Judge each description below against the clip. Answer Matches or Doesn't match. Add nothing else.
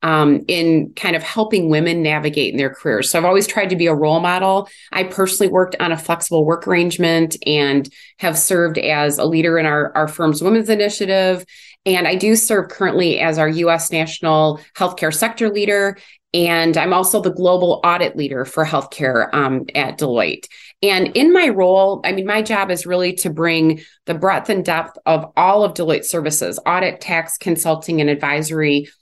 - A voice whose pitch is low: Doesn't match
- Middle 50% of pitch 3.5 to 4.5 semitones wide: Doesn't match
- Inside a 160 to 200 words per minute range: Matches